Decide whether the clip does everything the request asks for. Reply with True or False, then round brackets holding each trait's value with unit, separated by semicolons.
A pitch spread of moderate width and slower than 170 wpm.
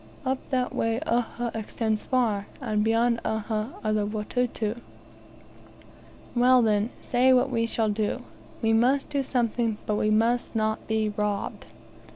False (2.3 semitones; 145 wpm)